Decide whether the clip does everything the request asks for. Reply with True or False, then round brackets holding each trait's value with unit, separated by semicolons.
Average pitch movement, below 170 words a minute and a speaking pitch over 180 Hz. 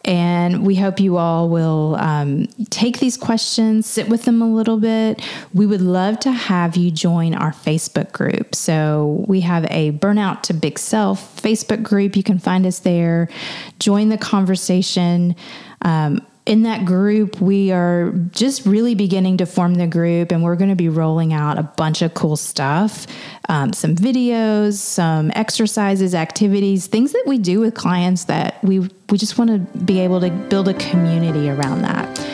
False (4.1 semitones; 175 wpm; 190 Hz)